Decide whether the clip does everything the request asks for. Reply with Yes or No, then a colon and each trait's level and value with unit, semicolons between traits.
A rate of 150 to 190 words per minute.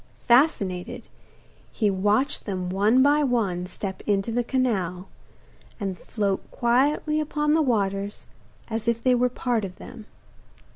No: slow, 135 wpm